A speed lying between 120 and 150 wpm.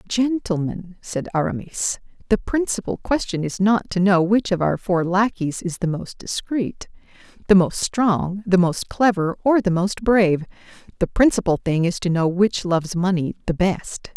No: average, 170 wpm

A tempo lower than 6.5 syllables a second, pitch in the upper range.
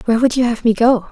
No: 7.3 syllables/s; high, 230 Hz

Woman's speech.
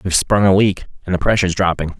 No: male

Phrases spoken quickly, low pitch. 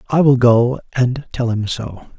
No: average, 190 wpm; low, 125 Hz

